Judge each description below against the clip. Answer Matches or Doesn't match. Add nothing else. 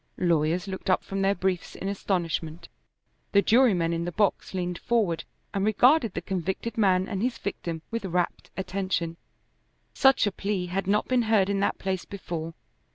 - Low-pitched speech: Doesn't match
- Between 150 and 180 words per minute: Matches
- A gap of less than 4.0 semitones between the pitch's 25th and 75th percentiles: Matches